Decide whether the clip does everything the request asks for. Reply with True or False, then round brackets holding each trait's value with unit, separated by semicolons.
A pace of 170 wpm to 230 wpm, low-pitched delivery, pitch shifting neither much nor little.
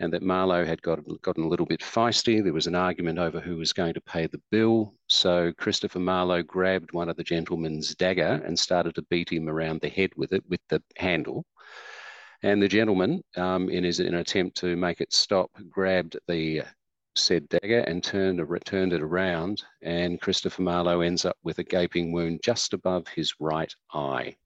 False (195 wpm; 90 Hz; 1.7 semitones)